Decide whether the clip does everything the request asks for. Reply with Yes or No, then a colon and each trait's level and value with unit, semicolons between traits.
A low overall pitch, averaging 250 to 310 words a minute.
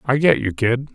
Yes: low, 125 Hz; fast, 255 wpm